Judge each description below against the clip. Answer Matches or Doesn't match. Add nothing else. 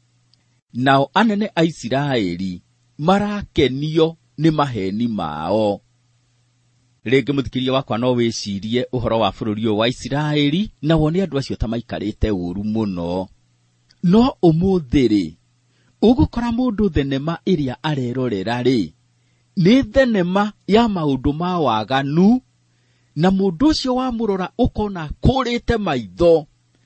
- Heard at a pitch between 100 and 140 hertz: Matches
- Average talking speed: Doesn't match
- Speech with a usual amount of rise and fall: Doesn't match